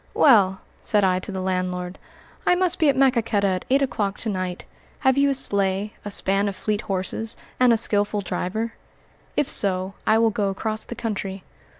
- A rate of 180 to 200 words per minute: Yes, average, 190 wpm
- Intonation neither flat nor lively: Yes, average, 3.2 semitones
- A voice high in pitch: Yes, high, 205 Hz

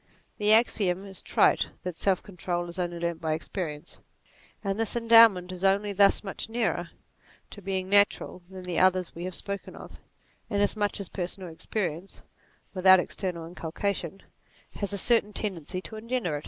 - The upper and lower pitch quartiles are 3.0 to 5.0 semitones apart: No, narrow, 2.5 semitones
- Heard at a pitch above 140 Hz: Yes, high, 190 Hz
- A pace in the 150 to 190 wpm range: Yes, average, 160 wpm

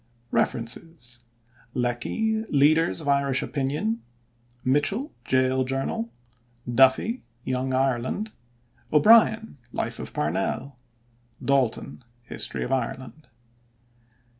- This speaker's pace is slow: Yes, slow, 85 wpm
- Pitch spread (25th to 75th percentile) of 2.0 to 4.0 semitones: No, average, 4.4 semitones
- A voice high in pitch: No, low, 135 Hz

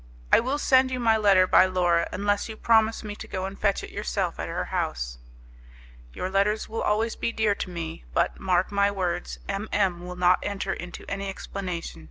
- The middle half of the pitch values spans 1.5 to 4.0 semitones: Yes, average, 3.0 semitones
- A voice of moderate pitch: No, high, 195 Hz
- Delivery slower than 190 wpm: No, fast, 205 wpm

